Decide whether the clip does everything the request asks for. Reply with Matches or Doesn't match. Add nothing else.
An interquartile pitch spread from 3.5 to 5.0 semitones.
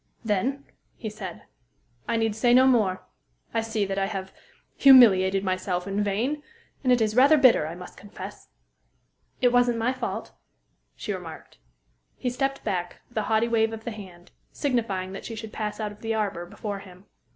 Matches